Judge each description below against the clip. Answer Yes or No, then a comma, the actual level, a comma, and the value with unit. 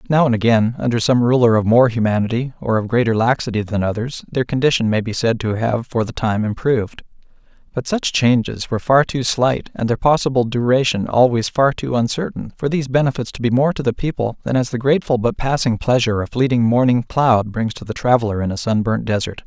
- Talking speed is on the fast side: Yes, fast, 215 wpm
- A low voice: Yes, low, 120 Hz